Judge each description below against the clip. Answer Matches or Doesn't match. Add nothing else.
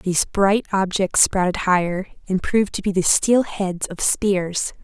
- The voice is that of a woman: Matches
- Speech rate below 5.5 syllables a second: Matches